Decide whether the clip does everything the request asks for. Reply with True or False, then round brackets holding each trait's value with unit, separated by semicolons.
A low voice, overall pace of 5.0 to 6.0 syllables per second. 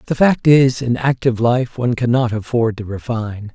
True (120 Hz; 5.3 syllables/s)